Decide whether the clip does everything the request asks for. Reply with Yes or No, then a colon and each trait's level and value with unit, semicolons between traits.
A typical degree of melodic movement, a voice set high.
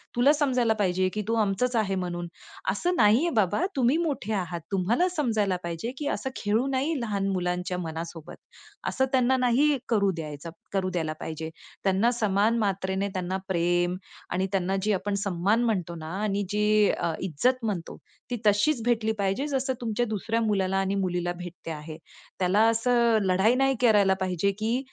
Yes: average, 4.6 semitones; high, 205 Hz